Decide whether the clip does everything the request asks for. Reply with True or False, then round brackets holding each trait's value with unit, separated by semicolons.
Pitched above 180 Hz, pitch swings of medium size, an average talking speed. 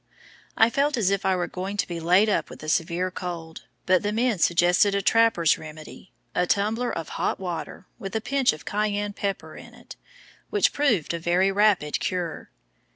True (190 Hz; 3.6 semitones; 190 wpm)